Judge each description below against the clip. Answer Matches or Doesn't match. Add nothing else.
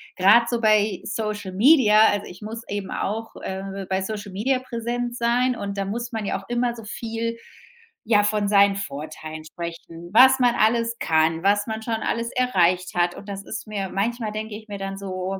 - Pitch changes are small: Doesn't match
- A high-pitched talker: Matches